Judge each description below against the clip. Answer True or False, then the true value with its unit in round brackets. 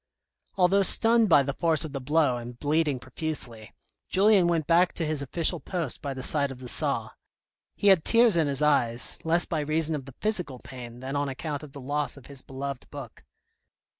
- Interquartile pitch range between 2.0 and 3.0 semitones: False (3.9 semitones)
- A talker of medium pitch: True (145 Hz)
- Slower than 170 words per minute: False (200 wpm)